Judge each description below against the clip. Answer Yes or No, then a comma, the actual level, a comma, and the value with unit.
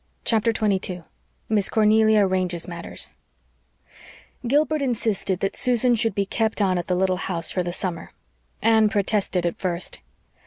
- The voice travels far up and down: No, average, 3.3 semitones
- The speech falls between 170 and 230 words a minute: No, average, 145 wpm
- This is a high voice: Yes, high, 200 Hz